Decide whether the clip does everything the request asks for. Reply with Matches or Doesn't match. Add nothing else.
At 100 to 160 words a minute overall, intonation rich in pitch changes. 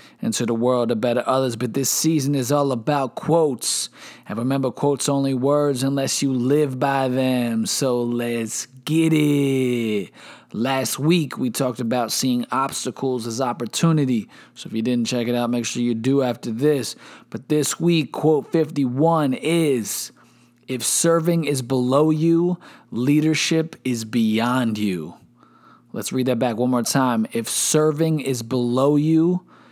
Doesn't match